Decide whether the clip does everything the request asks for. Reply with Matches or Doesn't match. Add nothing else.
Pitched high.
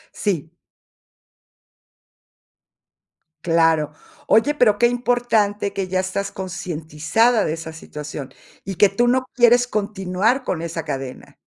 Matches